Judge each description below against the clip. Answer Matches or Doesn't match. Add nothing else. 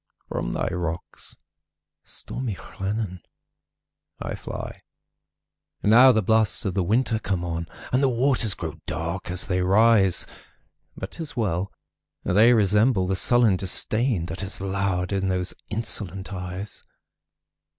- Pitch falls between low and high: Doesn't match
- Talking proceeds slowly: Matches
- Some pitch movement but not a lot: Matches